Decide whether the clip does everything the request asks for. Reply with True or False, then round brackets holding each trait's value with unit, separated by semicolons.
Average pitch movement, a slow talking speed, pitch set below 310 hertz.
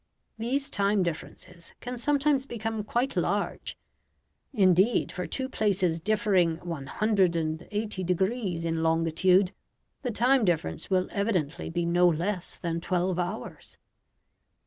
True (4.4 semitones; 115 wpm; 185 Hz)